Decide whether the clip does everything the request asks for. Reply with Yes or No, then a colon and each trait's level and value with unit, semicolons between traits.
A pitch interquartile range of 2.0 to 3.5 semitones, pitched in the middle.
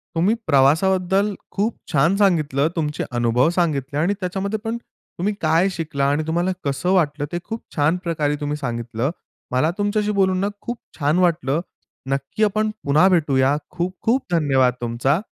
No: average, 5.2 semitones; medium, 165 Hz